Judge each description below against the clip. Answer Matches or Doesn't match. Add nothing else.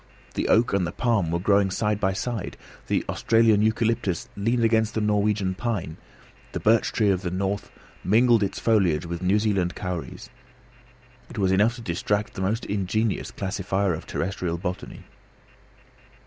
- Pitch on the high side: Doesn't match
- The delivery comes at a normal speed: Matches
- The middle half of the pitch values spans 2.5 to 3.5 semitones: Matches